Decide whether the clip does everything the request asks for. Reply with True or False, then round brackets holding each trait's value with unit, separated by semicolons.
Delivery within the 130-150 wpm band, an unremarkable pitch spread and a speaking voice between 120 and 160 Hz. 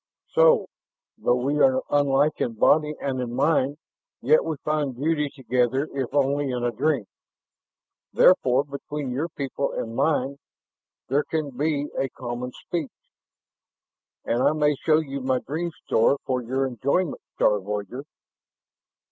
True (140 wpm; 3.0 semitones; 140 Hz)